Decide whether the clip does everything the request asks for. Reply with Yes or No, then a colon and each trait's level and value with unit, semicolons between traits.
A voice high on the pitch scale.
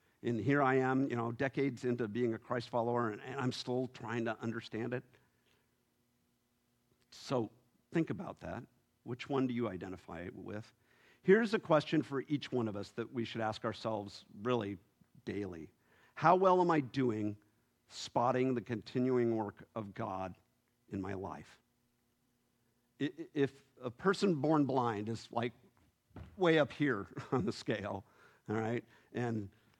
No: low, 120 Hz